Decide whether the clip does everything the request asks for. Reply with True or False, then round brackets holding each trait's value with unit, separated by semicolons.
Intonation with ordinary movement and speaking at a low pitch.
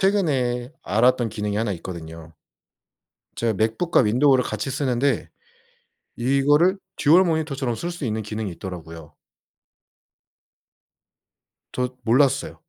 True (5.0 semitones; 125 Hz)